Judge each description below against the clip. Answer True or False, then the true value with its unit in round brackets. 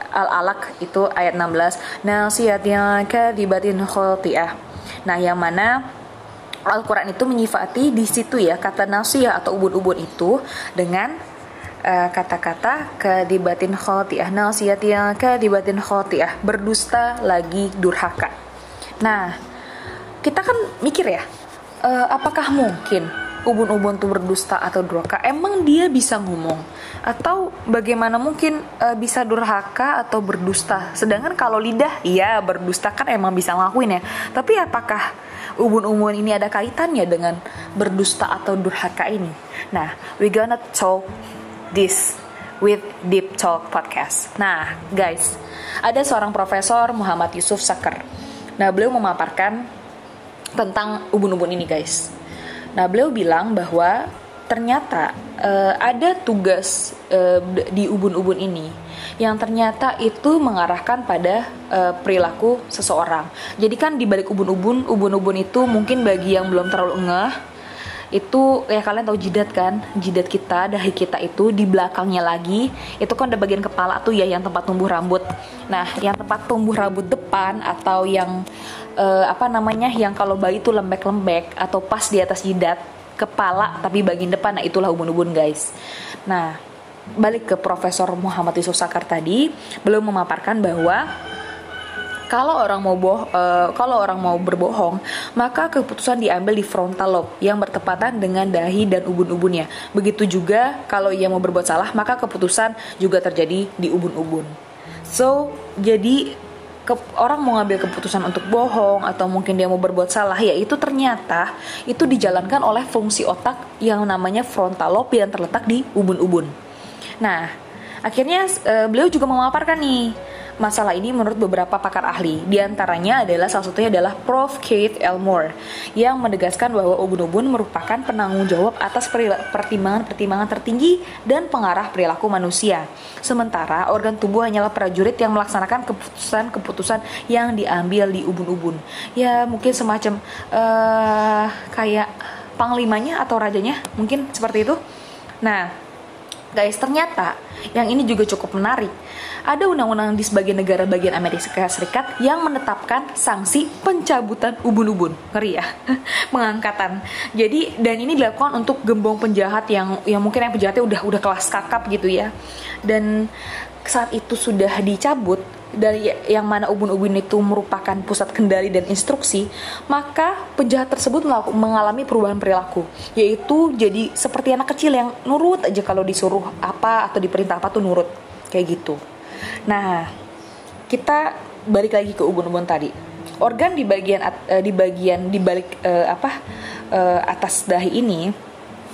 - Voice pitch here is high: True (205 Hz)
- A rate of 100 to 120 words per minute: False (135 wpm)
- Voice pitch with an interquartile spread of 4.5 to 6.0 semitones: False (3.9 semitones)